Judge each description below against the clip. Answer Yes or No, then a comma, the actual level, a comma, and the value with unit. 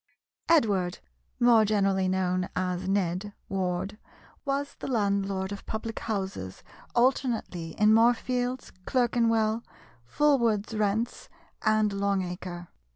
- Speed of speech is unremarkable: No, slow, 100 wpm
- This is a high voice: Yes, high, 205 Hz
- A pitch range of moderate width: Yes, average, 3.6 semitones